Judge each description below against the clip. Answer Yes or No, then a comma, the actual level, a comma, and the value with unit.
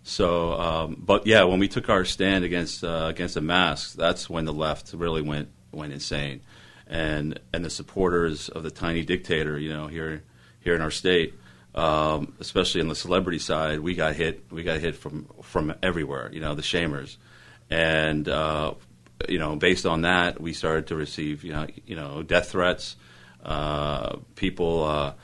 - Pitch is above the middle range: No, very low, 80 Hz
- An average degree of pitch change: No, narrow, 2.1 semitones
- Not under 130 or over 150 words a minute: No, average, 180 wpm